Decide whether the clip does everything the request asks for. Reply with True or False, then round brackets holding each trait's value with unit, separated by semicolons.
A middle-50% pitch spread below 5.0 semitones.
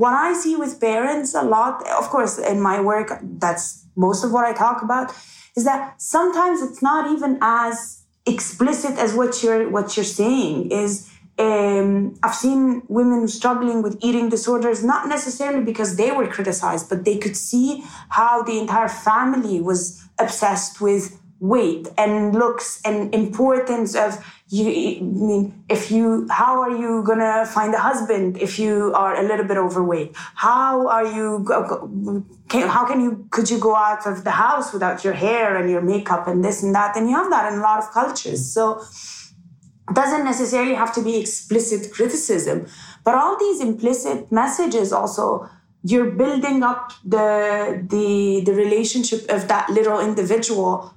True (3.3 semitones)